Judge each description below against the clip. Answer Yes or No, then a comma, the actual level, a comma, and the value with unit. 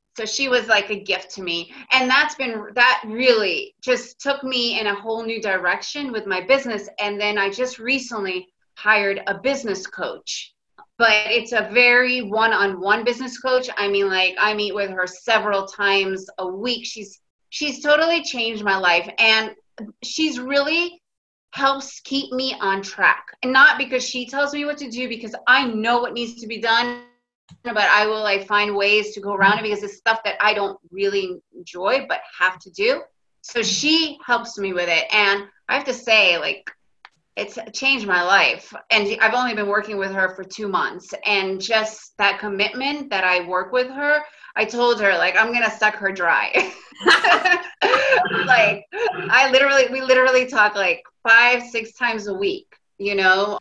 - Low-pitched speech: No, high, 225 Hz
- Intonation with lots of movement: No, average, 4.2 semitones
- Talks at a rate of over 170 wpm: Yes, average, 185 wpm